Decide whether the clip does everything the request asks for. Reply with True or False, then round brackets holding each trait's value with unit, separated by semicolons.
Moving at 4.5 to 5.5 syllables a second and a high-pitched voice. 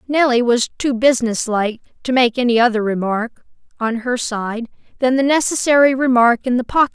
True (5.4 syllables/s; 245 Hz)